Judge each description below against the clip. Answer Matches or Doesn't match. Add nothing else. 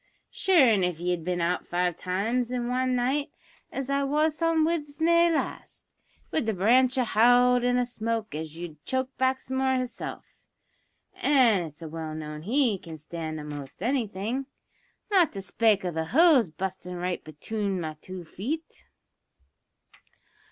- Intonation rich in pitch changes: Matches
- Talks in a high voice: Matches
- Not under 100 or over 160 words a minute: Matches